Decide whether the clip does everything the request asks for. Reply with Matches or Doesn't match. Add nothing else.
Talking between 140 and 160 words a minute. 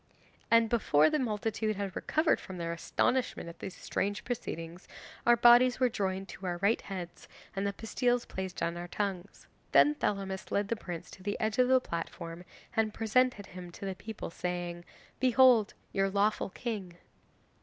Doesn't match